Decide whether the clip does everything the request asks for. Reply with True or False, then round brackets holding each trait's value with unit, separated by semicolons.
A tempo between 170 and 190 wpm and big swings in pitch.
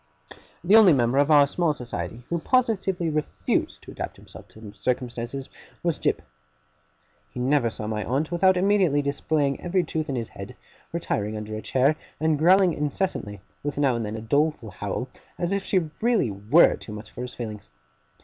True (180 wpm; 6.8 semitones)